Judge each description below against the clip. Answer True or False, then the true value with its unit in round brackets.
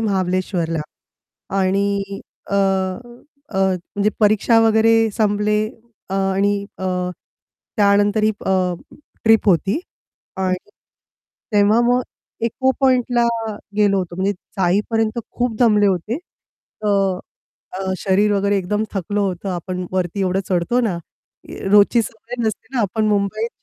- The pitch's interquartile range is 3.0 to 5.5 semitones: False (2.6 semitones)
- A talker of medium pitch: False (205 Hz)